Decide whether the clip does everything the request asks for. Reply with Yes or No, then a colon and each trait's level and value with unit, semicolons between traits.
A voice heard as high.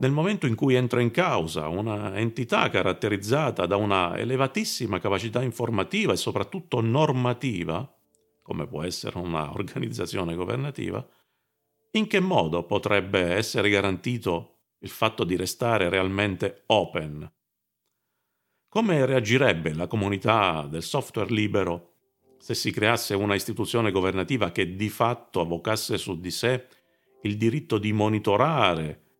No: low, 110 Hz